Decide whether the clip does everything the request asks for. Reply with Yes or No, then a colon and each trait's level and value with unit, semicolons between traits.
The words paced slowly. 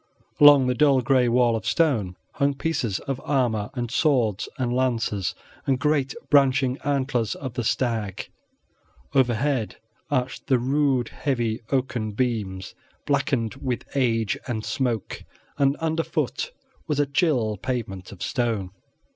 Yes: slow, 130 wpm